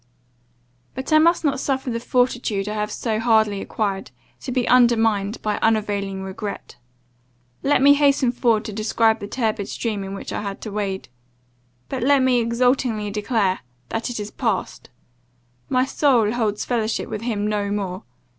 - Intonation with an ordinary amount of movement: Yes, average, 3.3 semitones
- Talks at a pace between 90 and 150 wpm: No, average, 165 wpm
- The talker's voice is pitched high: Yes, high, 220 Hz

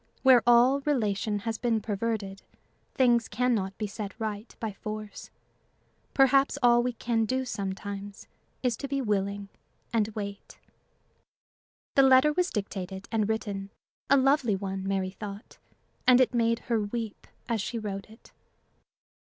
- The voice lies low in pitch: No, high, 220 Hz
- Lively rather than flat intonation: No, average, 3.4 semitones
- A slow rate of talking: No, average, 145 wpm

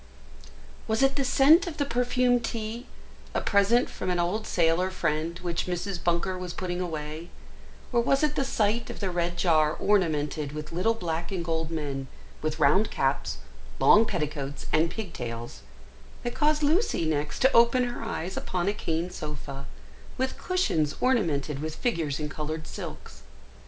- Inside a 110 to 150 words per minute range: No, average, 160 wpm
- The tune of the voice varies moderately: No, wide, 7.0 semitones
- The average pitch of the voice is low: No, medium, 175 Hz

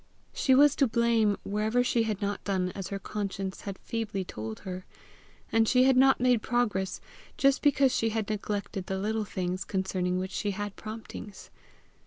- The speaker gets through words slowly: No, average, 175 wpm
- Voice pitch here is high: Yes, high, 210 Hz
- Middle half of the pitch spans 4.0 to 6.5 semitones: No, average, 3.4 semitones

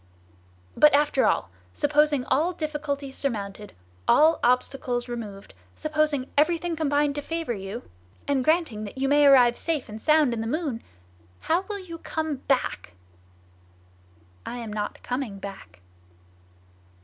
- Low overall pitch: No, very high, 280 Hz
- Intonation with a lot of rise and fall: No, average, 4.5 semitones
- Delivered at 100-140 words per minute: Yes, slow, 135 wpm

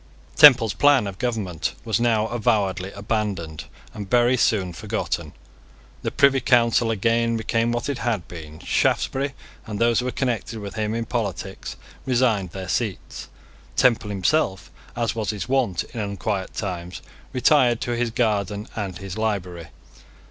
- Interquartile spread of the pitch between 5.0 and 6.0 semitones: No, average, 3.6 semitones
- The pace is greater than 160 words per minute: No, average, 150 wpm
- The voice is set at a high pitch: No, low, 110 Hz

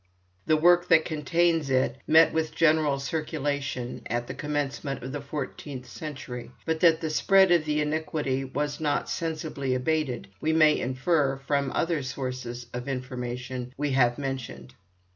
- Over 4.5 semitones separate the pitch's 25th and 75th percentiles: No, average, 3.4 semitones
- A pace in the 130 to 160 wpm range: Yes, average, 150 wpm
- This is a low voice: No, medium, 145 Hz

